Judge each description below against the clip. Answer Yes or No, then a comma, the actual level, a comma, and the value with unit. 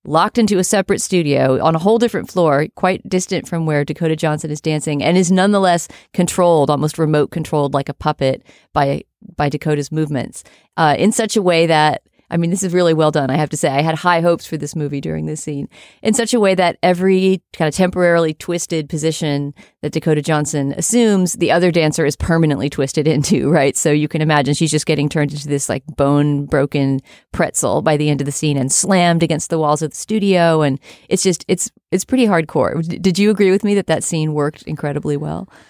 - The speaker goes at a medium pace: No, fast, 215 wpm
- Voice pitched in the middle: Yes, medium, 160 Hz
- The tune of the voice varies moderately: Yes, average, 3.7 semitones